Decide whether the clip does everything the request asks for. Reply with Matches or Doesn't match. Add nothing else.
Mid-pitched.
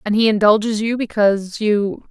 Doesn't match